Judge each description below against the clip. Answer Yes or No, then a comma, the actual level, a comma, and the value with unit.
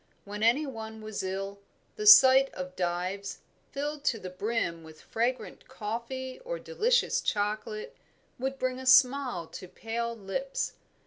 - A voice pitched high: Yes, high, 235 Hz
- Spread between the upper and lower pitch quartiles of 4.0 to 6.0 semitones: Yes, average, 5.1 semitones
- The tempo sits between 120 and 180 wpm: Yes, average, 140 wpm